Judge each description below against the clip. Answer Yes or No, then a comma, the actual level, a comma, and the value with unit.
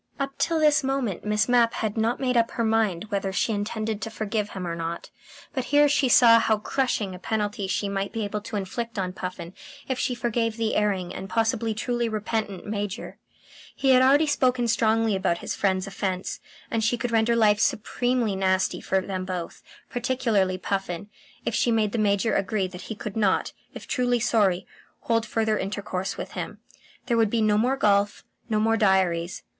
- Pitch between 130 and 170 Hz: No, high, 215 Hz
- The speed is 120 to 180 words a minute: No, average, 190 wpm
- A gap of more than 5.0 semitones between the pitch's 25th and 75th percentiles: No, average, 3.2 semitones